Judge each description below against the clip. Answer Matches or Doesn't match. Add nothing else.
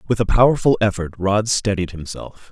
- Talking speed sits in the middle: Matches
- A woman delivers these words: Doesn't match